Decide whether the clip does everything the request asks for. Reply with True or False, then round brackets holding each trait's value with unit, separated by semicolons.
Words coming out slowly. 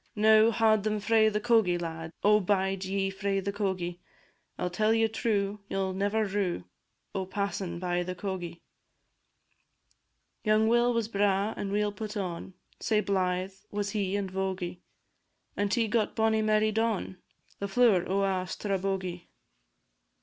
False (155 wpm)